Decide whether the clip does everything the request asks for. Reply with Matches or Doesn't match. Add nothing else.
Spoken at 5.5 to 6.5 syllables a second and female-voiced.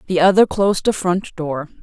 Doesn't match